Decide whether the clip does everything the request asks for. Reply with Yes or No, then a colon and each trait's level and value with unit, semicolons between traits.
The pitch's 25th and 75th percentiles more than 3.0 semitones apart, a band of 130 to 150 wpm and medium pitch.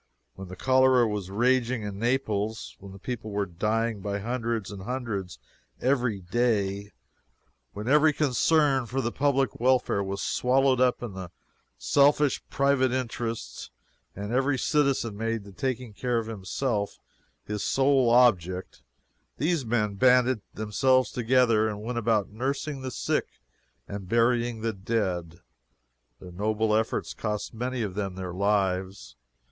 No: average, 4.1 semitones; average, 140 wpm; low, 115 Hz